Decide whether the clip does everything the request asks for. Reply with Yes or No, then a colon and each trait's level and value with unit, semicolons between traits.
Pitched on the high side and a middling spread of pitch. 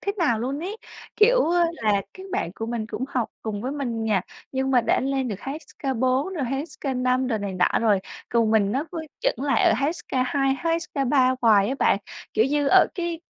Yes: very high, 260 Hz; average, 4.4 semitones